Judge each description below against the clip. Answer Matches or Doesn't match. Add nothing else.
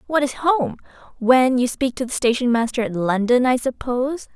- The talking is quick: Doesn't match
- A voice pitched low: Doesn't match